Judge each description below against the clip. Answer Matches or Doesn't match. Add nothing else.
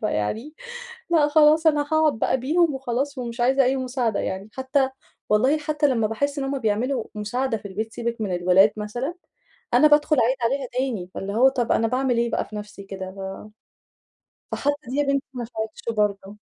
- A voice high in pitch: Matches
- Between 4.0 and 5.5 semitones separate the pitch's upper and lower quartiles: Matches